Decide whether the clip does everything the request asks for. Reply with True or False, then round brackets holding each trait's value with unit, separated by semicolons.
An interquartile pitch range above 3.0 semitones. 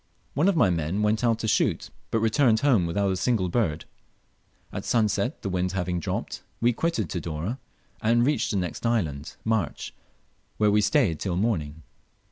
True (4.8 semitones)